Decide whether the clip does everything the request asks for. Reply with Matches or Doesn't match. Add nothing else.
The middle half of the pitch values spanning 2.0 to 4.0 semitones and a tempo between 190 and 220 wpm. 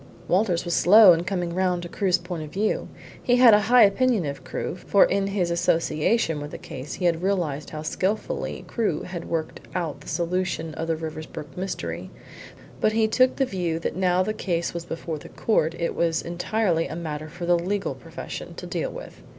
Matches